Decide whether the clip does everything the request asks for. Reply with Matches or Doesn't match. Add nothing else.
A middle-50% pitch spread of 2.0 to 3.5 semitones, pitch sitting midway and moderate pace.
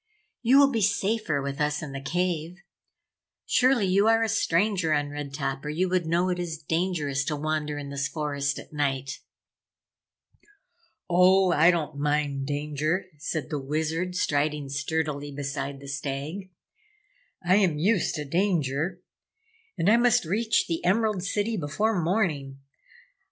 Doesn't match